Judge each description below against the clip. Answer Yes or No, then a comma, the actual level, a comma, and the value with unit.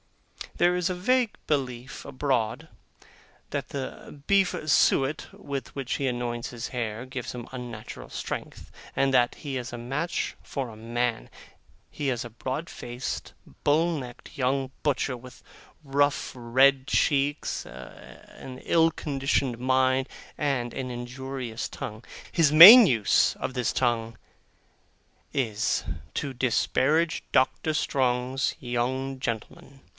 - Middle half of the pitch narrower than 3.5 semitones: Yes, average, 2.7 semitones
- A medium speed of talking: No, slow, 125 wpm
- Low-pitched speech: Yes, low, 130 Hz